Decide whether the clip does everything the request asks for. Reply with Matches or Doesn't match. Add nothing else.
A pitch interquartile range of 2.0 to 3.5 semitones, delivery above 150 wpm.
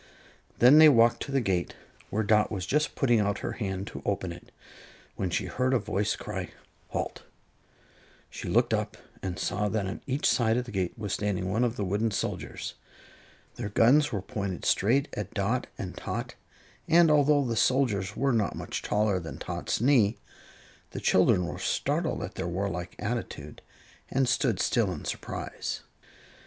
Doesn't match